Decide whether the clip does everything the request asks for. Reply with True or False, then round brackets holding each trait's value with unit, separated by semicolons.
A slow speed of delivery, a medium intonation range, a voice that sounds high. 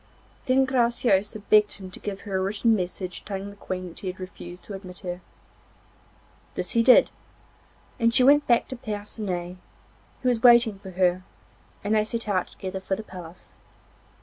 False (175 wpm; 3.8 semitones; 200 Hz)